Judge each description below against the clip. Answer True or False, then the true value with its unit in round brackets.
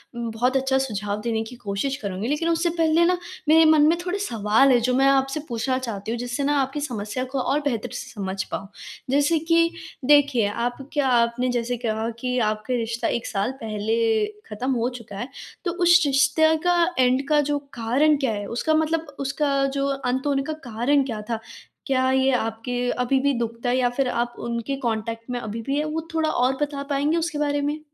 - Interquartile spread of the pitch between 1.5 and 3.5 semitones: False (3.9 semitones)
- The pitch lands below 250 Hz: False (260 Hz)